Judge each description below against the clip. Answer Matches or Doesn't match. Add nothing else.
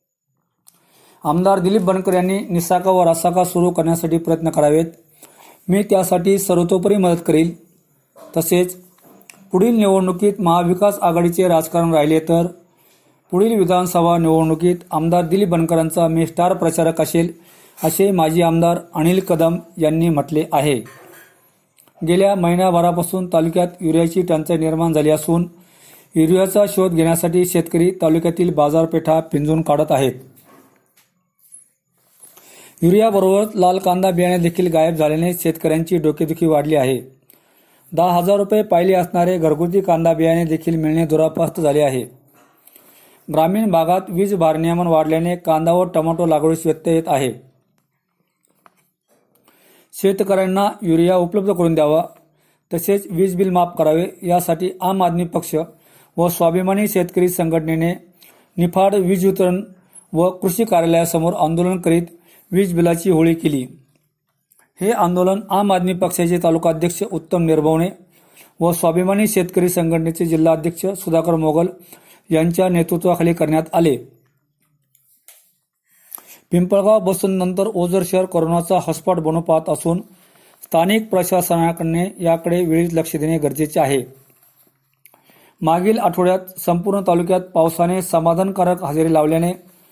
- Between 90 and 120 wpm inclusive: Matches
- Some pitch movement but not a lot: Doesn't match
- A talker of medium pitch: Matches